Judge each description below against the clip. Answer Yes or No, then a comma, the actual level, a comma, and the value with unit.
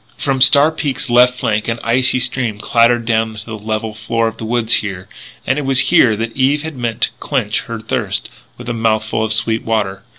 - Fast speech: Yes, fast, 210 wpm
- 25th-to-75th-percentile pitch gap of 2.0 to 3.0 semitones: Yes, narrow, 2.5 semitones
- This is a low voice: Yes, low, 115 Hz